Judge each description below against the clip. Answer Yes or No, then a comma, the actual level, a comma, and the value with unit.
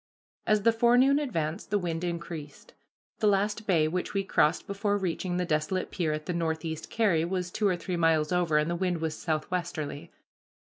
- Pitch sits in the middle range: Yes, medium, 175 Hz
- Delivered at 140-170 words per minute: No, average, 185 wpm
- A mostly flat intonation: No, average, 3.7 semitones